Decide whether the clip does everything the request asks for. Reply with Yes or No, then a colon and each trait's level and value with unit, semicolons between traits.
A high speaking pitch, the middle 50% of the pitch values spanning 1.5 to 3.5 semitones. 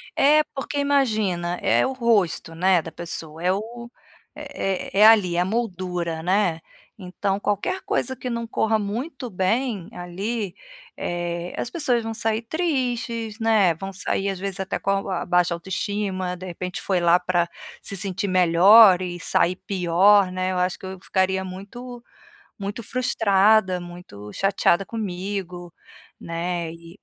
No: high, 195 Hz; average, 3.9 semitones